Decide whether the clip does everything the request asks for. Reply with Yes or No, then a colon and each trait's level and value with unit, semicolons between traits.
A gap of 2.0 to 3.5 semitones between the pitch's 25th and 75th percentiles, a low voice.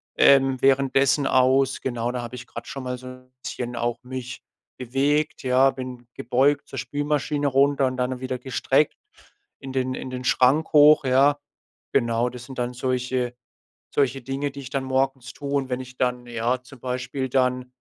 No: narrow, 1.4 semitones; low, 130 Hz